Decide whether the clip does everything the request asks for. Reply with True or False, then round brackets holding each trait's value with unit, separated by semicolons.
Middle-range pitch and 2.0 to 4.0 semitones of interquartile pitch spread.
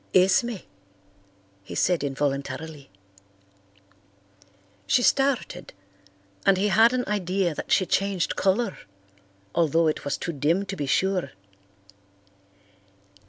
False (180 Hz; 4.8 semitones)